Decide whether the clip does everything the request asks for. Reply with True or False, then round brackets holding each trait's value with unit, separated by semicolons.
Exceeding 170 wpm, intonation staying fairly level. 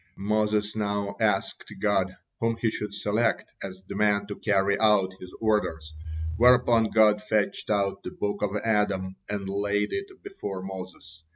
False (155 wpm; 1.7 semitones)